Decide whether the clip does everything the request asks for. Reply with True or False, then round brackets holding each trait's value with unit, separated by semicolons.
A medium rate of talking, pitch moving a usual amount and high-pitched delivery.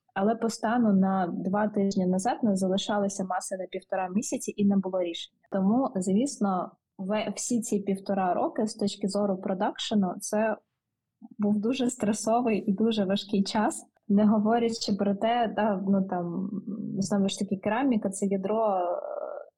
False (145 wpm; 2.3 semitones; 205 Hz)